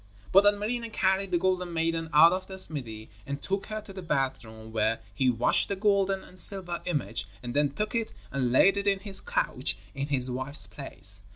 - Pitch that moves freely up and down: Yes, wide, 6.7 semitones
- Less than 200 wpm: No, fast, 205 wpm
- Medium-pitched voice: Yes, medium, 170 Hz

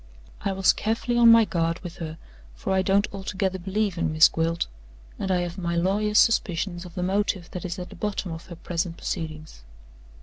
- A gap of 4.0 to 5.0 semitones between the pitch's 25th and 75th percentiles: No, average, 2.9 semitones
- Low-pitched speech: No, medium, 180 Hz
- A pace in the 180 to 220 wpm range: Yes, average, 200 wpm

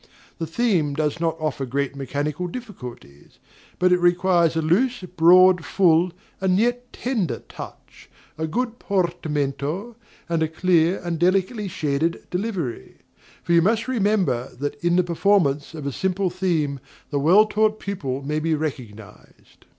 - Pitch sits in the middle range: Yes, medium, 170 Hz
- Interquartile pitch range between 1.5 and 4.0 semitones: No, average, 4.4 semitones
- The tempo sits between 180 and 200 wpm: No, average, 145 wpm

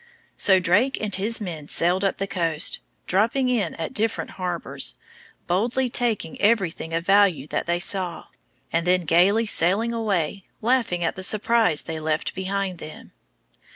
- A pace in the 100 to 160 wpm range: Yes, average, 155 wpm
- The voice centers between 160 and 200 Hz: Yes, high, 190 Hz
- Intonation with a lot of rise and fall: No, average, 4.2 semitones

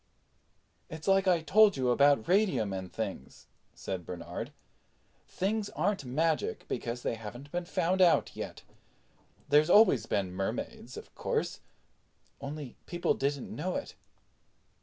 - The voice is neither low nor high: Yes, medium, 145 Hz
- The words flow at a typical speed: No, slow, 130 wpm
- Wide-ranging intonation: Yes, wide, 8.2 semitones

